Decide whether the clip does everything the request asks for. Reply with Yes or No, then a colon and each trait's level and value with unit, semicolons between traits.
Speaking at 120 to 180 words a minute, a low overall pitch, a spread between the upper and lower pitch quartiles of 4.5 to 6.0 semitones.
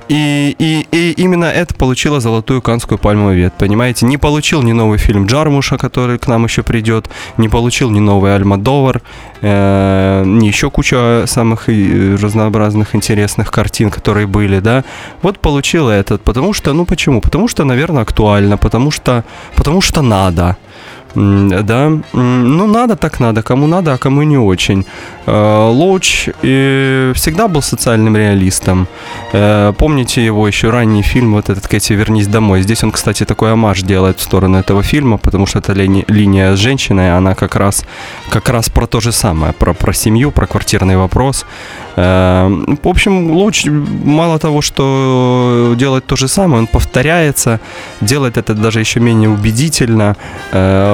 Yes: average, 155 wpm; low, 115 Hz; average, 4.9 semitones